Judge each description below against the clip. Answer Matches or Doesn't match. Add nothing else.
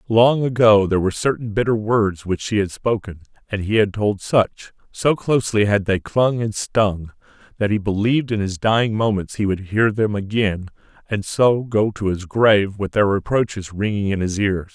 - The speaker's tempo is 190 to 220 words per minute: Matches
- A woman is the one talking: Doesn't match